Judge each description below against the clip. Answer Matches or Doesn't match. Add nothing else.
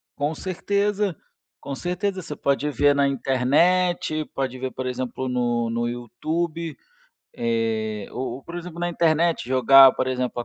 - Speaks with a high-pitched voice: Doesn't match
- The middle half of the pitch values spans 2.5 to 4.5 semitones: Doesn't match